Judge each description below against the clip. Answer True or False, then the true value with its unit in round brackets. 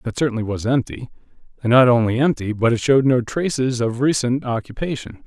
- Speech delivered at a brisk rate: False (170 wpm)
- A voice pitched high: False (120 Hz)